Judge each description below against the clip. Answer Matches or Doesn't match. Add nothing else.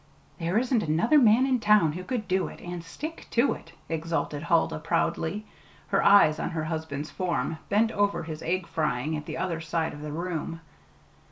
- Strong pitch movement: Doesn't match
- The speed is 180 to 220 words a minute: Matches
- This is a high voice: Doesn't match